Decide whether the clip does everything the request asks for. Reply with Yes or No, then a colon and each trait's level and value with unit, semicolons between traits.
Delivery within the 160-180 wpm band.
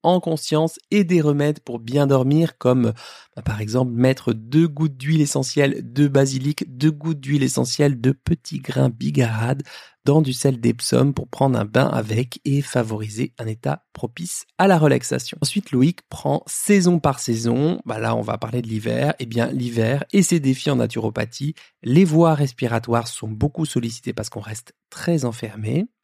Yes: average, 175 wpm